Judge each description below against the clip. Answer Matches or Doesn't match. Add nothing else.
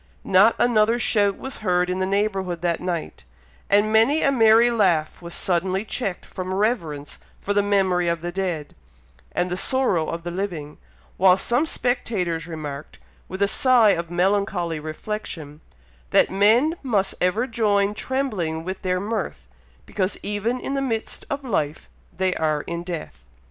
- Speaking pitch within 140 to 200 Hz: Matches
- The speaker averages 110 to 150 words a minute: Doesn't match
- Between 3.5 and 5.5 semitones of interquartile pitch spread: Matches